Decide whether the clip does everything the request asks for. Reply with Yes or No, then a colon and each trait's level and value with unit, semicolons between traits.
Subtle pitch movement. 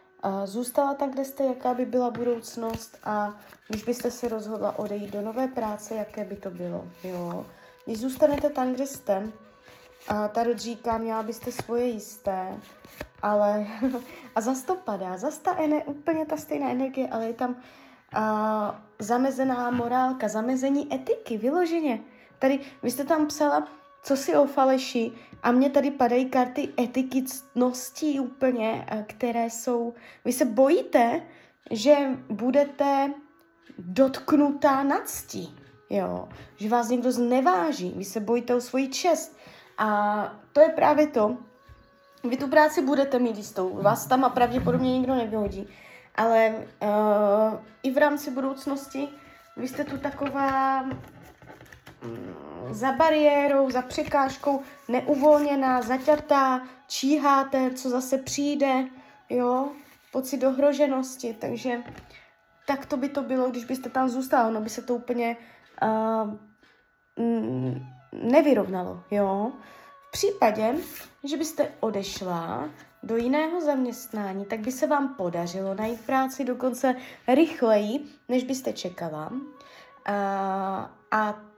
No: average, 4.2 semitones